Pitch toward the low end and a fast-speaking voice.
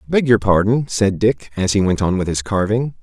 Yes: low, 105 Hz; fast, 240 wpm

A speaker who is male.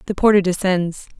No: female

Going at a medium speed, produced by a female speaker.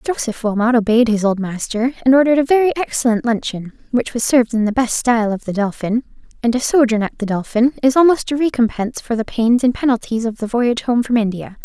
No: fast, 220 wpm; female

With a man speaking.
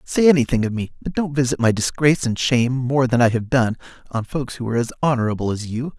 Yes: male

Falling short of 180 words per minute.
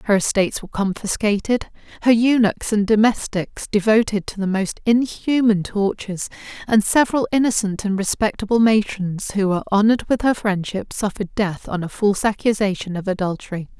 Yes: average, 150 wpm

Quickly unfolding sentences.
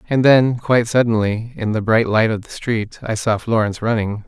Yes: fast, 210 wpm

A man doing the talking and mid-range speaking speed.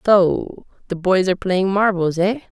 No: female; average, 165 wpm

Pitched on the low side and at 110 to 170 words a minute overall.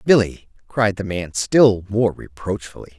Yes: low, 100 Hz; average, 140 wpm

